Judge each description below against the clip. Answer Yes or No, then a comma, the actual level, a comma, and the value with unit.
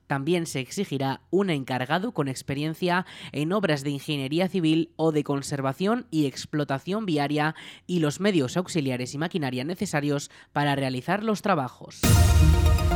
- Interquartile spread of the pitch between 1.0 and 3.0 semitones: No, average, 4.5 semitones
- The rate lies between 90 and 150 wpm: Yes, average, 135 wpm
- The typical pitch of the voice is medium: Yes, medium, 150 Hz